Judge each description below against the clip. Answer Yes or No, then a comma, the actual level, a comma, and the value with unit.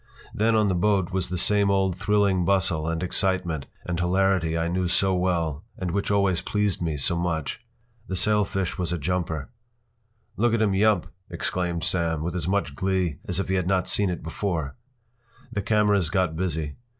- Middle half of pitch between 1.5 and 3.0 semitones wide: Yes, average, 2.7 semitones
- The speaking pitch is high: No, very low, 90 Hz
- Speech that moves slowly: No, average, 185 wpm